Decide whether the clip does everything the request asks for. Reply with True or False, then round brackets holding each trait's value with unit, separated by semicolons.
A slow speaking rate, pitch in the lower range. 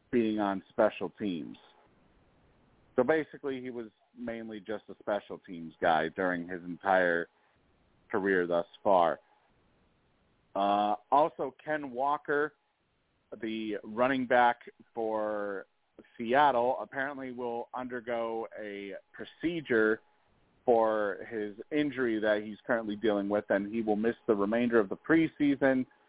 True (115 wpm; 115 Hz)